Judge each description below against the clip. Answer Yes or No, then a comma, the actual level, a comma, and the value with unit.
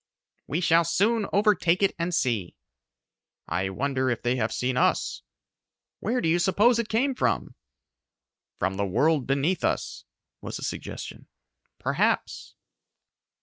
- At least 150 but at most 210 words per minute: No, slow, 135 wpm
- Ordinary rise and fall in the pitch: No, wide, 8.4 semitones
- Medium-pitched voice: Yes, medium, 165 Hz